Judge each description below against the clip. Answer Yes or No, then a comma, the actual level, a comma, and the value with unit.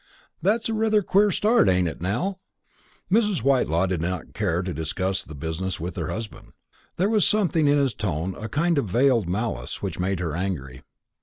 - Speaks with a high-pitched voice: No, low, 100 Hz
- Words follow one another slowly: No, average, 185 wpm